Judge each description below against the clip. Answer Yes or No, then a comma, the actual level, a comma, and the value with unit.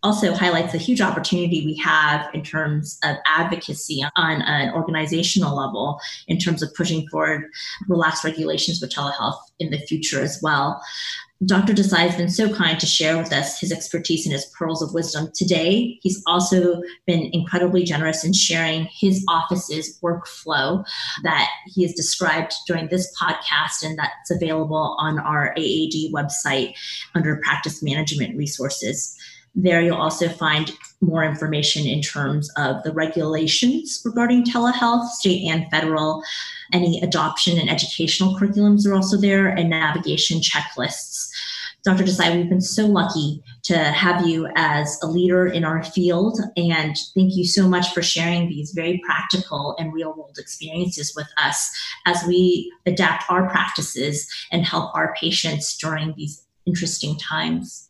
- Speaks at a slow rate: No, average, 150 wpm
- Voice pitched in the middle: Yes, medium, 165 Hz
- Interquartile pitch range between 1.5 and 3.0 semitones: Yes, narrow, 2.6 semitones